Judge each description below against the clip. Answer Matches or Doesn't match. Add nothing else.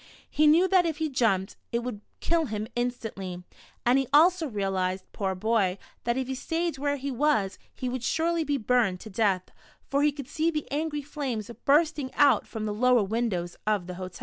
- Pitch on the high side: Matches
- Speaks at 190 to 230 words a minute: Matches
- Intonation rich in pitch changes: Matches